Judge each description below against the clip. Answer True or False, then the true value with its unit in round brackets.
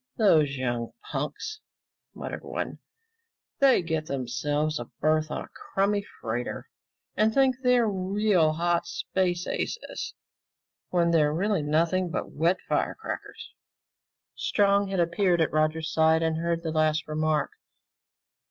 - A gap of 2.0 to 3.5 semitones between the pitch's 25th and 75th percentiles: False (4.0 semitones)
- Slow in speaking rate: True (125 wpm)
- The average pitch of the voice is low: False (165 Hz)